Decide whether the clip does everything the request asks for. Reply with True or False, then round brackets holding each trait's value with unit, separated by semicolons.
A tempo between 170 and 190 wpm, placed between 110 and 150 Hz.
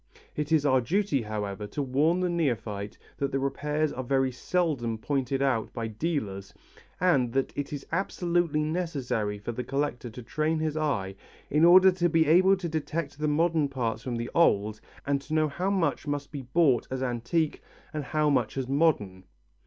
True (180 wpm; 140 Hz)